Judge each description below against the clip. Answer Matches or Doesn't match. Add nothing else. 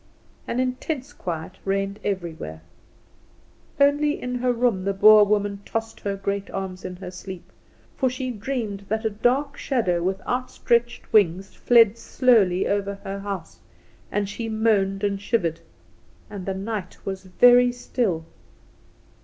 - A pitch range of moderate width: Matches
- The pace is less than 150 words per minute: Matches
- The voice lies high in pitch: Matches